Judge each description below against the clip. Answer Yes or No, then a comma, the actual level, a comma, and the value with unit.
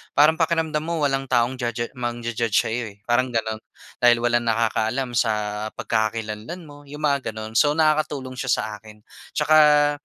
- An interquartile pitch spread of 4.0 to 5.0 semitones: Yes, average, 4.4 semitones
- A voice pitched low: Yes, low, 125 Hz